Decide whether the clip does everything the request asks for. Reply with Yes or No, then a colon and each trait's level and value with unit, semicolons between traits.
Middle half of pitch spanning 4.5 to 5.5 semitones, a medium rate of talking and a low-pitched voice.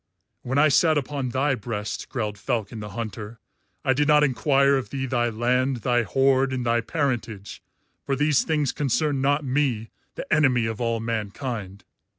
No: average, 3.4 semitones; average, 165 wpm; low, 125 Hz